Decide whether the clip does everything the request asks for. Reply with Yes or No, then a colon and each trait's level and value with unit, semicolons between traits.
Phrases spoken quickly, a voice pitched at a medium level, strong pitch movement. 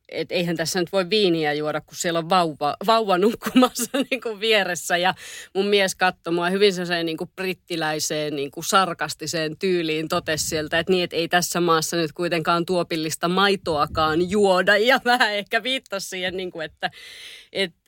No: fast, 165 wpm; medium, 175 Hz; average, 3.2 semitones